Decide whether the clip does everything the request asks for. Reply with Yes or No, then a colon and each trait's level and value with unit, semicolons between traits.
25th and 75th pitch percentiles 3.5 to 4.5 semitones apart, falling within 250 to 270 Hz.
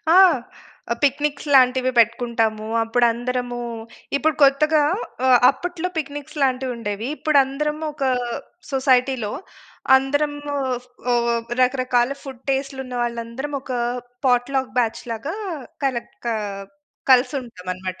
No: average, 2.7 semitones; very high, 260 Hz